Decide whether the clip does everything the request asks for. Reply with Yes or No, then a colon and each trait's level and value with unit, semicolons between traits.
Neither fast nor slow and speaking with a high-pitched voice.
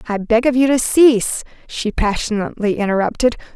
Yes: average, 150 wpm; high, 230 Hz